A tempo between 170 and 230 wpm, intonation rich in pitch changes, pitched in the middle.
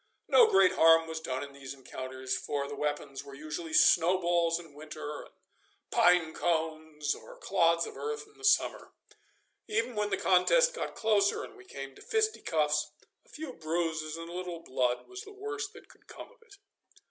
Yes: average, 180 wpm; wide, 6.6 semitones; medium, 165 Hz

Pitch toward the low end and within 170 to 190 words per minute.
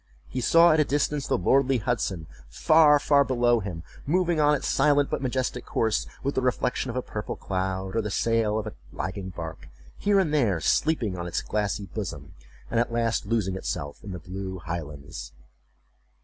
Yes: low, 115 Hz; average, 185 wpm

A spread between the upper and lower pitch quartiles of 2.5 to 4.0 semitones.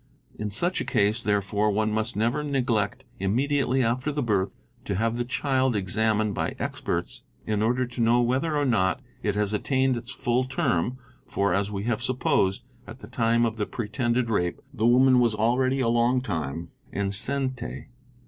Yes: average, 3.6 semitones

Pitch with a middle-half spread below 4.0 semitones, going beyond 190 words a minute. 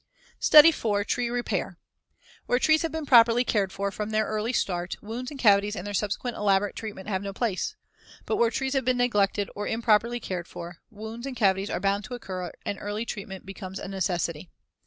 Yes: average, 3.6 semitones; average, 200 wpm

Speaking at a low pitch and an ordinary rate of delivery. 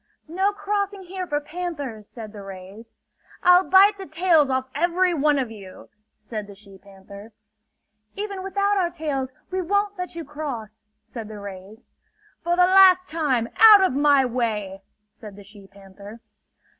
No: very high, 285 Hz; average, 160 wpm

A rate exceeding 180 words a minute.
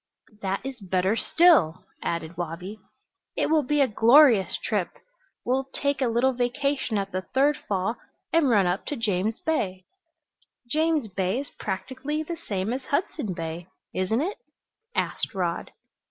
No: average, 150 wpm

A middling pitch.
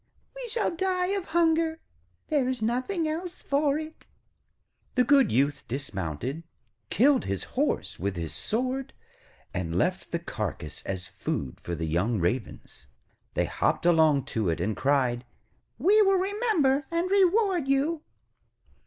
No: very high, 255 Hz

